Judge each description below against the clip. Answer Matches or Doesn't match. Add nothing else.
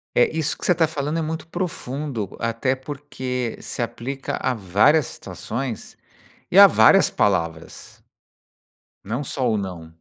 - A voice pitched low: Matches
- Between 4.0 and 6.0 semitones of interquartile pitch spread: Matches